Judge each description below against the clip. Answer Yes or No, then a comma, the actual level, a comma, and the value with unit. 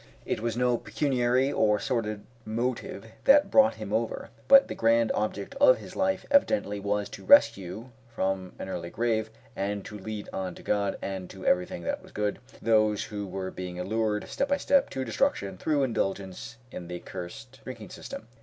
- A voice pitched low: Yes, low, 110 Hz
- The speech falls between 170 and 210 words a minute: Yes, average, 180 wpm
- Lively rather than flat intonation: No, average, 4.2 semitones